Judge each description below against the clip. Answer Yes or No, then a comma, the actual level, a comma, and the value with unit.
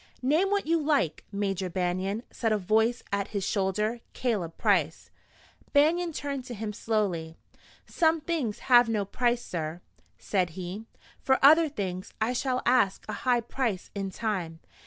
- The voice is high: Yes, high, 220 Hz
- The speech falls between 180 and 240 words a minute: No, average, 155 wpm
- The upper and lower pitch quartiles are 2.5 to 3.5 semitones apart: No, average, 5.3 semitones